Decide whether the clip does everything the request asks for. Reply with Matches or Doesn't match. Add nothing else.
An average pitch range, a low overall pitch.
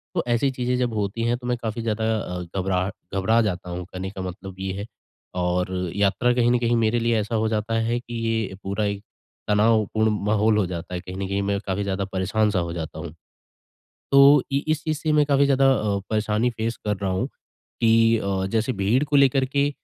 Matches